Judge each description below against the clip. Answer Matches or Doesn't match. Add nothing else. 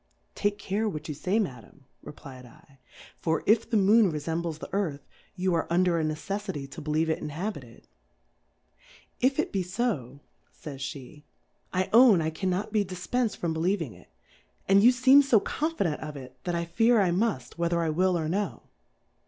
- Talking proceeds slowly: Doesn't match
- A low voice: Doesn't match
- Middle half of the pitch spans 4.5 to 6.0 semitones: Matches